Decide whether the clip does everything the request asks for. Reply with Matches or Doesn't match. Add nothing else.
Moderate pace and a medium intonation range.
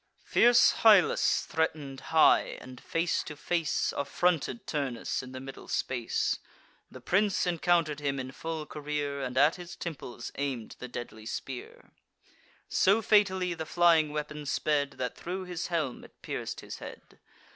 Matches